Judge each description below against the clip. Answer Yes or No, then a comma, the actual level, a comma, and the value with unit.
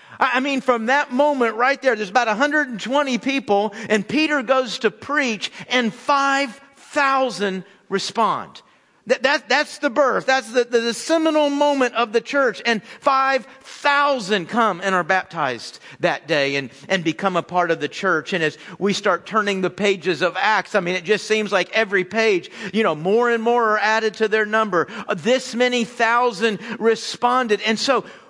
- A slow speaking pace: No, average, 175 wpm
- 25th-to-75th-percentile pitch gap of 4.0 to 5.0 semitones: Yes, average, 4.7 semitones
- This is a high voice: Yes, high, 230 Hz